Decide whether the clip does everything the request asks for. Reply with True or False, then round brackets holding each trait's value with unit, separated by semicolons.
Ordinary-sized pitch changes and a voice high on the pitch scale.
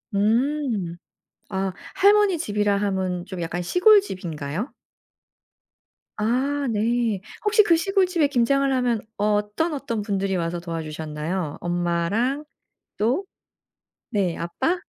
False (8.0 semitones; 210 Hz)